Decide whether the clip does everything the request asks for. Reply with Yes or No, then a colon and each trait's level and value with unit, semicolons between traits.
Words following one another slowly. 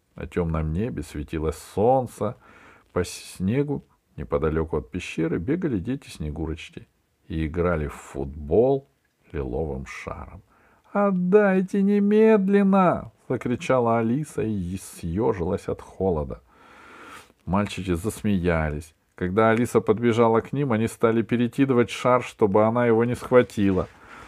Yes: slow, 105 wpm